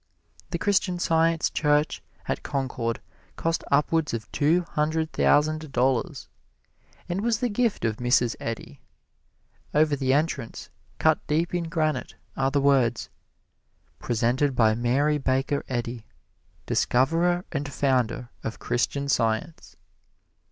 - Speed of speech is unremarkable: No, slow, 120 wpm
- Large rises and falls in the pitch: No, average, 4.7 semitones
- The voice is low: No, medium, 145 Hz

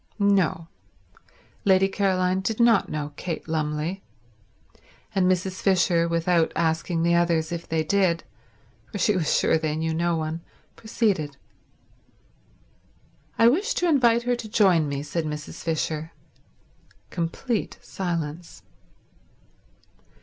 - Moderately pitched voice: Yes, medium, 170 Hz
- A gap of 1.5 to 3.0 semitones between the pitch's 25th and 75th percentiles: No, average, 3.5 semitones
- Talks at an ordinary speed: No, slow, 120 wpm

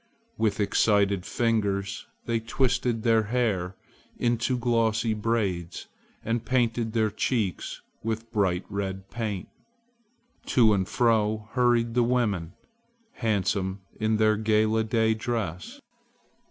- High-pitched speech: No, low, 110 Hz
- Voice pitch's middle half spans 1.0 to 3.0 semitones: Yes, narrow, 2.6 semitones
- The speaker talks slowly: Yes, slow, 110 wpm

